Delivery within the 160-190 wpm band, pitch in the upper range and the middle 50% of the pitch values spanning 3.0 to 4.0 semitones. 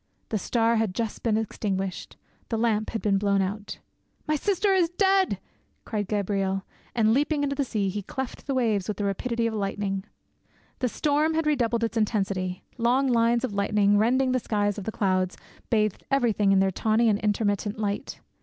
Yes: average, 180 wpm; high, 220 Hz; average, 3.6 semitones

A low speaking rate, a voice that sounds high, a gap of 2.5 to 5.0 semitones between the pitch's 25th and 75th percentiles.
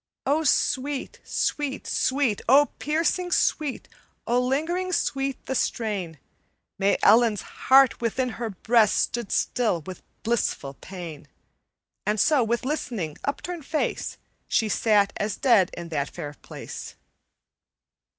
No: slow, 120 wpm; high, 235 Hz; wide, 5.6 semitones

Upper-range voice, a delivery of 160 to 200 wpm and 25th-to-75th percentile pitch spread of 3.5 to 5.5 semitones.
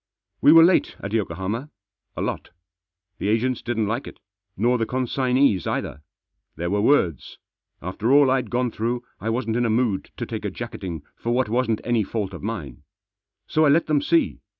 No: low, 115 Hz; average, 185 wpm; average, 3.9 semitones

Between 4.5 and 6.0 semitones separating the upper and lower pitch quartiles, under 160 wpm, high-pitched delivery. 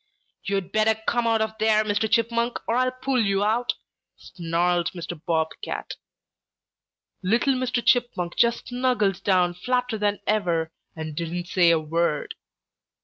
Yes: average, 5.1 semitones; average, 145 wpm; high, 210 Hz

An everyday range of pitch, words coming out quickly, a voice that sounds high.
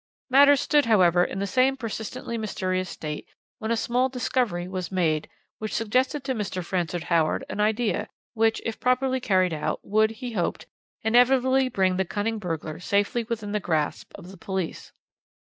No: average, 5.0 semitones; average, 165 wpm; high, 210 Hz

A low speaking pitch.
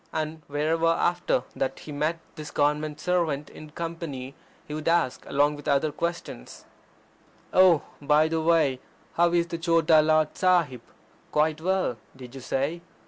No: medium, 155 Hz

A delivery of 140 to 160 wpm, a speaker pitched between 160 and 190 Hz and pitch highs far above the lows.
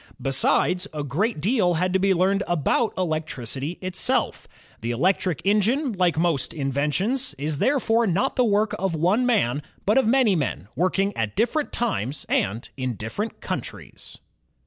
Yes: average, 150 wpm; medium, 185 Hz; wide, 6.8 semitones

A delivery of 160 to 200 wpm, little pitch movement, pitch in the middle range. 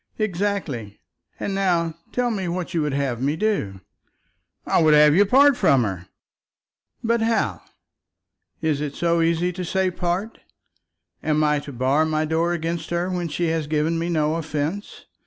No: average, 165 wpm; average, 3.6 semitones; medium, 165 Hz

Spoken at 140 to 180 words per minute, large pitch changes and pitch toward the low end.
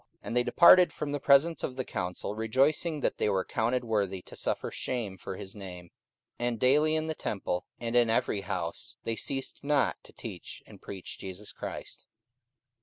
No: average, 190 wpm; wide, 6.0 semitones; low, 120 Hz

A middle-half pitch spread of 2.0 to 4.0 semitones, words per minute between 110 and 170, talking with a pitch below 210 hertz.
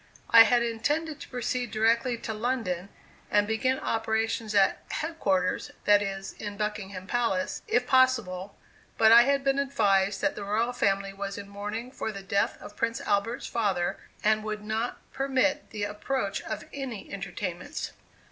No: average, 3.5 semitones; average, 160 wpm; high, 220 Hz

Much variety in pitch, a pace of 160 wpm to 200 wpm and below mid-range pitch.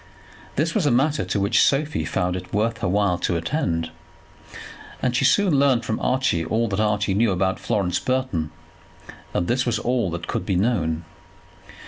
Yes: wide, 6.2 semitones; average, 175 wpm; low, 105 Hz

